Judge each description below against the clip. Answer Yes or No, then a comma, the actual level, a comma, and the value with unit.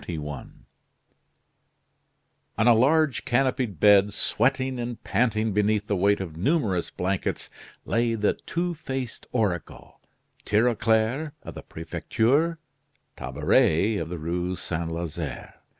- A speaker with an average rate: No, slow, 115 wpm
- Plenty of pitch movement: Yes, wide, 6.1 semitones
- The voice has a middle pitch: No, low, 110 Hz